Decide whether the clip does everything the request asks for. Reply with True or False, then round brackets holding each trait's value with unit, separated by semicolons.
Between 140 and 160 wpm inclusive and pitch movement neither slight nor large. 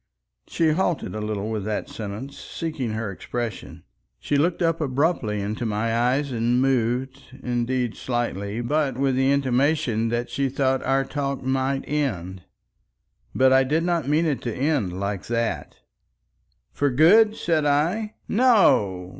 True (145 wpm; 4.4 semitones)